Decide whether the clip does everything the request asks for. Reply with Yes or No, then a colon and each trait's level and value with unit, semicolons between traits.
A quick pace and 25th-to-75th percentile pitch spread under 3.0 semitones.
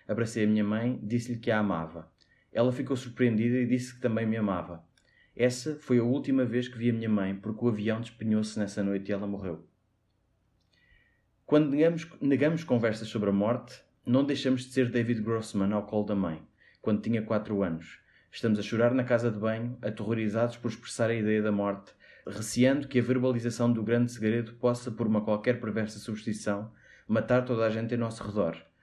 Yes: fast, 190 wpm; narrow, 2.5 semitones